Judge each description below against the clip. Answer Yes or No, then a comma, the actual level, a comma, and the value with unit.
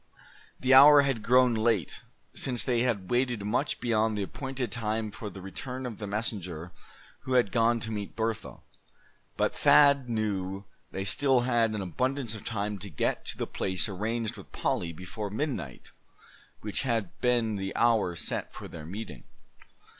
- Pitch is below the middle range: Yes, low, 110 Hz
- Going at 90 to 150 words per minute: No, average, 165 wpm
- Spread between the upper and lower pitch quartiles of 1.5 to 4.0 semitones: Yes, average, 3.7 semitones